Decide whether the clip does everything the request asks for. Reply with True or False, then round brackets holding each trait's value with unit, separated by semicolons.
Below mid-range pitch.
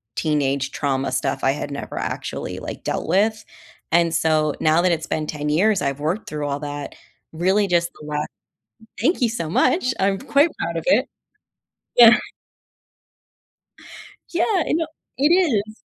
False (170 Hz)